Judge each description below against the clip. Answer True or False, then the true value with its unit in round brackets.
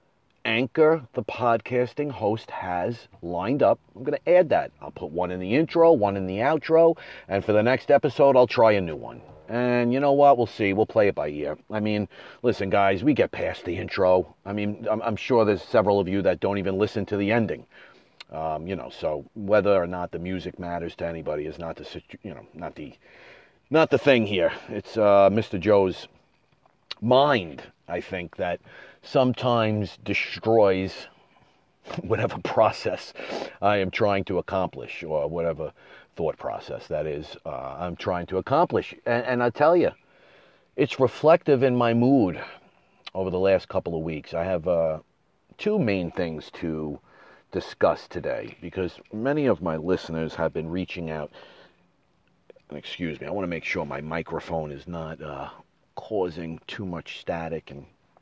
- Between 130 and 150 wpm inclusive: False (175 wpm)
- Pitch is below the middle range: True (100 Hz)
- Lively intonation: True (5.7 semitones)